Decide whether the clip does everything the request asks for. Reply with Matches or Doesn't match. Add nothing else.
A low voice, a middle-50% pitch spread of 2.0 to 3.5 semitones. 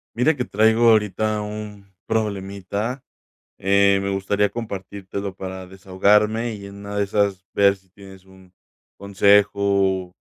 Doesn't match